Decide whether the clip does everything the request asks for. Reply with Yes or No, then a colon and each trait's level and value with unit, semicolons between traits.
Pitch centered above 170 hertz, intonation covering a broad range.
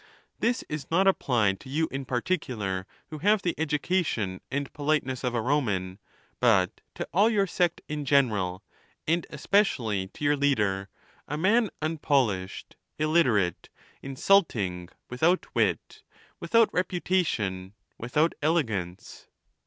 No: medium, 140 Hz; wide, 8.3 semitones